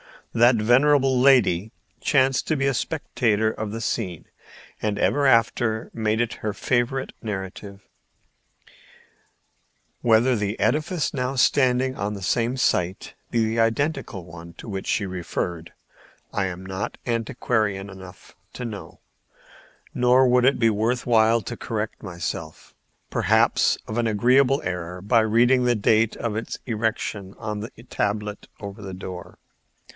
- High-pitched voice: No, low, 110 Hz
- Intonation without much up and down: No, average, 3.6 semitones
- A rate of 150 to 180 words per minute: No, average, 140 wpm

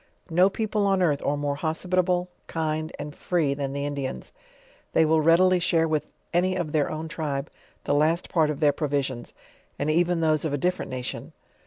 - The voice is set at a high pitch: No, medium, 155 Hz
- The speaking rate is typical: Yes, average, 185 wpm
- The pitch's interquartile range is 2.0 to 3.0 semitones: No, average, 3.4 semitones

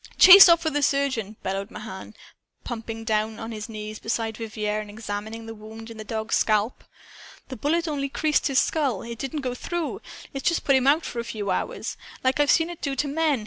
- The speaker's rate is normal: No, fast, 215 wpm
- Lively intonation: No, average, 4.7 semitones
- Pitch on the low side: No, high, 230 Hz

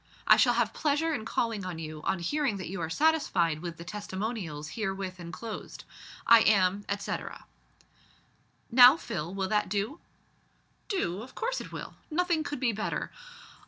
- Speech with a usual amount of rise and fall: No, wide, 5.9 semitones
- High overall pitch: Yes, high, 210 Hz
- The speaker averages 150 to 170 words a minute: Yes, average, 160 wpm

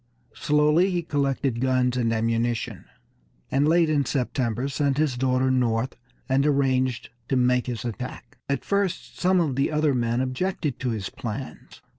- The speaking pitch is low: Yes, low, 130 Hz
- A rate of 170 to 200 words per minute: No, average, 155 wpm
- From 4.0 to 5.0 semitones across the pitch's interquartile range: No, average, 3.2 semitones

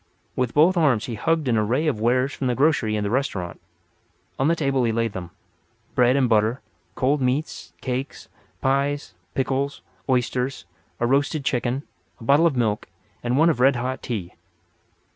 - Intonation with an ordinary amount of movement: Yes, average, 3.2 semitones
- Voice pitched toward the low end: Yes, low, 130 Hz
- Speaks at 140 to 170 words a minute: Yes, average, 165 wpm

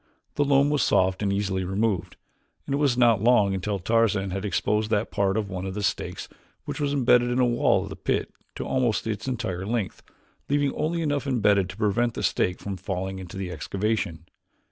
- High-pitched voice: No, low, 105 Hz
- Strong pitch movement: No, average, 4.2 semitones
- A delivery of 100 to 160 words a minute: No, fast, 205 wpm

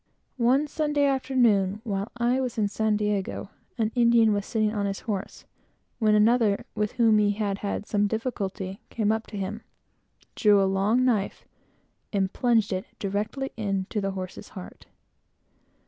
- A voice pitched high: Yes, high, 210 Hz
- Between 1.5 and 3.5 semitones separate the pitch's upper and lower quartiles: Yes, average, 2.8 semitones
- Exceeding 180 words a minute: No, average, 155 wpm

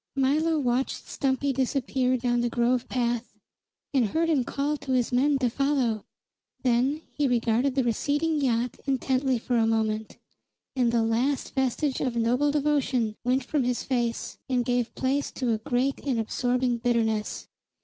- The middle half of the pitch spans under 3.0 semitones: Yes, narrow, 2.5 semitones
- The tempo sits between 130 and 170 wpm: Yes, average, 160 wpm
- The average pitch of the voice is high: Yes, very high, 250 Hz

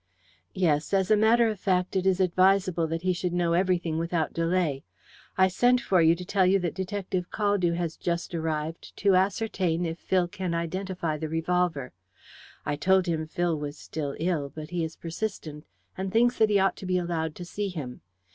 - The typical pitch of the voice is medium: Yes, medium, 180 Hz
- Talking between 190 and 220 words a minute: Yes, average, 195 wpm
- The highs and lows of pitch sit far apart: No, average, 2.7 semitones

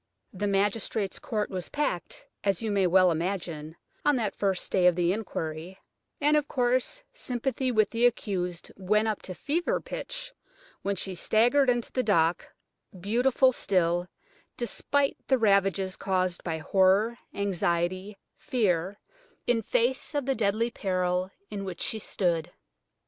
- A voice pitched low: No, high, 200 Hz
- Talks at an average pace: Yes, average, 145 wpm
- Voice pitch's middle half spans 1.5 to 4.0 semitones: No, average, 4.8 semitones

